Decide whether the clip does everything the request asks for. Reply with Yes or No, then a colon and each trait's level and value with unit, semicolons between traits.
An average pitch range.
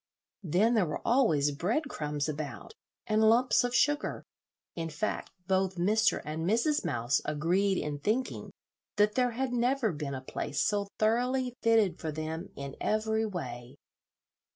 No: wide, 7.1 semitones